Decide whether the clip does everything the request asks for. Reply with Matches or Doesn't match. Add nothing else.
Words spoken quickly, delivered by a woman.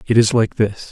Doesn't match